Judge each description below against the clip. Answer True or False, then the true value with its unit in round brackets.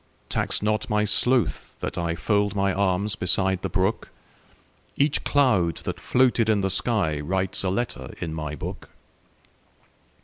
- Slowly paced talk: True (130 wpm)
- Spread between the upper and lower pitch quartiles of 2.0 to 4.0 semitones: True (3.0 semitones)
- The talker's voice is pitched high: False (100 Hz)